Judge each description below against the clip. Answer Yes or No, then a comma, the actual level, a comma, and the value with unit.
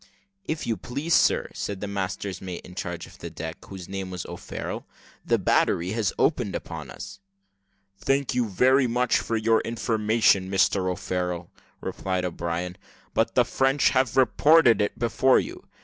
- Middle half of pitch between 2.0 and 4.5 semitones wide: No, average, 5.2 semitones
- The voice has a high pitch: No, low, 100 Hz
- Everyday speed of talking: Yes, average, 160 wpm